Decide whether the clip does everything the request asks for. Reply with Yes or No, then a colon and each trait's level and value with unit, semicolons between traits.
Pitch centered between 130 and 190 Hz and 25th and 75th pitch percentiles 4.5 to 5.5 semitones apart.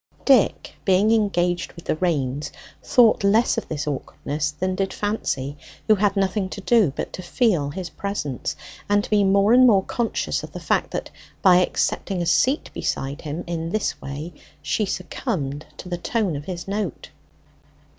Yes: medium, 185 Hz; average, 4.9 semitones